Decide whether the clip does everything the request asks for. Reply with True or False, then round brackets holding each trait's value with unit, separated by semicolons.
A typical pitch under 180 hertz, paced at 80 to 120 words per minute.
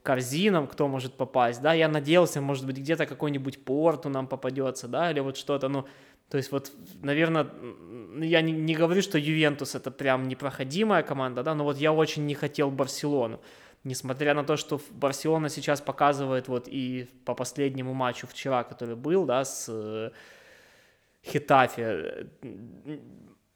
False (140 Hz; 150 wpm)